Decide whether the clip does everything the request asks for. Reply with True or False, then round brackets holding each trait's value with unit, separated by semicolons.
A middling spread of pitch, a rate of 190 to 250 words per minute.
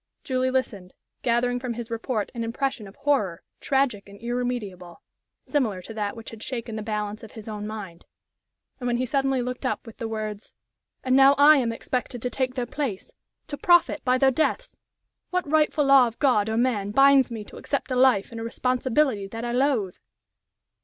True (3.5 semitones; 195 wpm)